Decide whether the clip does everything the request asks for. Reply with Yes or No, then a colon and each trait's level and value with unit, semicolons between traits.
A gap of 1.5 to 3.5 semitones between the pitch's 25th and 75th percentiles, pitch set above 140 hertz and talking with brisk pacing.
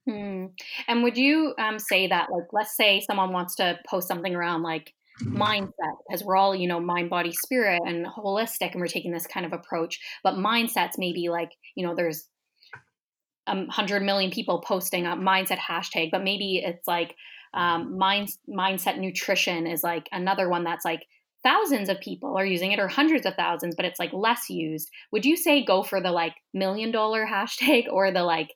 No: average, 2.7 semitones; high, 190 Hz; average, 195 wpm